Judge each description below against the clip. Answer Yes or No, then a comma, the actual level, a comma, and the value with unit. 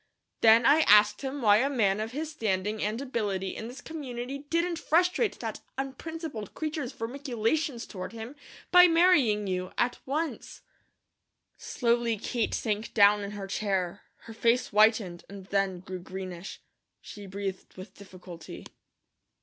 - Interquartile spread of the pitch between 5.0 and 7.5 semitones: Yes, wide, 5.5 semitones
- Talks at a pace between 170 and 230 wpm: No, average, 140 wpm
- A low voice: No, high, 225 Hz